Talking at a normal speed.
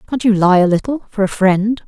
No: fast, 255 wpm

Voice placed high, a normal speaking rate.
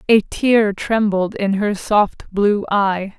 Yes: high, 205 Hz; average, 150 wpm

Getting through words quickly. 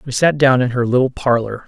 Yes: fast, 250 wpm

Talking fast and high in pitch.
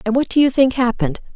Yes: fast, 265 wpm; high, 245 Hz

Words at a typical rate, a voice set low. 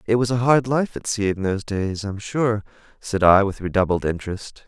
No: fast, 230 wpm; low, 105 Hz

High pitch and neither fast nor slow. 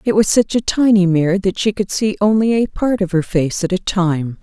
No: high, 195 Hz; fast, 255 wpm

